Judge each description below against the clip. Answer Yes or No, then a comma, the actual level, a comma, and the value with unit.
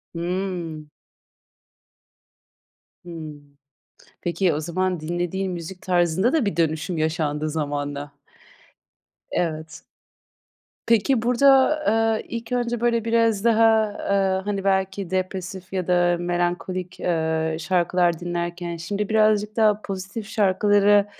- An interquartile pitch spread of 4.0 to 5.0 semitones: No, average, 3.5 semitones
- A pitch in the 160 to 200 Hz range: Yes, medium, 185 Hz